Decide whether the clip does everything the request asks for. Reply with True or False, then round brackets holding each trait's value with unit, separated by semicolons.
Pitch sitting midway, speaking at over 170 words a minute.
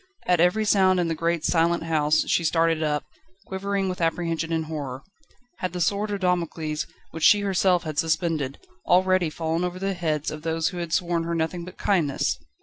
True (170 Hz; 190 wpm)